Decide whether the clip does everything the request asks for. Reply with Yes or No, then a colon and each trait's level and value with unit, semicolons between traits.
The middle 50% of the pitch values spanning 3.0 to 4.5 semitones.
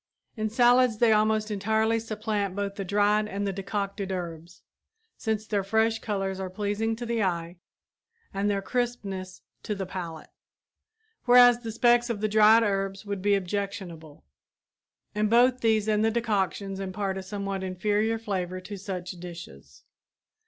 No: narrow, 2.4 semitones